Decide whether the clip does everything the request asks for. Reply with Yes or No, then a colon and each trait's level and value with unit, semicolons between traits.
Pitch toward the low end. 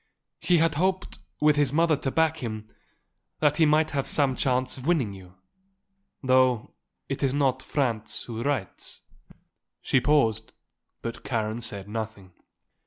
Yes: low, 130 Hz